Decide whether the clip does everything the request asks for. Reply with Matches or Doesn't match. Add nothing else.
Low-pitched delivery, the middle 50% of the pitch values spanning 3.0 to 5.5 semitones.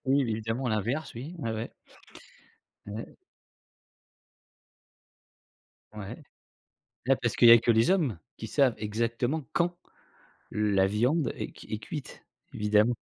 Matches